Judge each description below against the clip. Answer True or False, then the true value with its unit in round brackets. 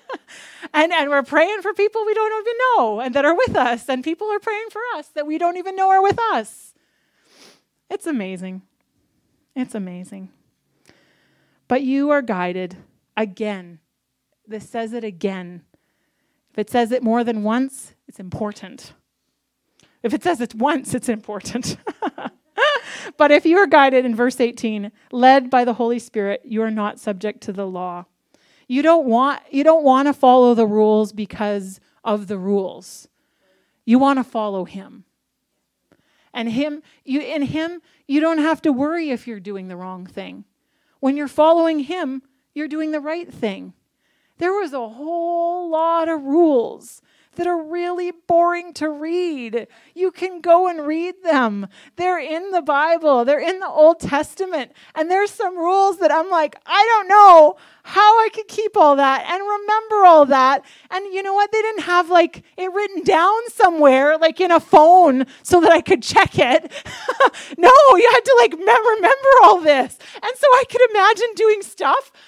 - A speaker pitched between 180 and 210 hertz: False (305 Hz)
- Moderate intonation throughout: False (6.9 semitones)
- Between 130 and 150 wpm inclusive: False (170 wpm)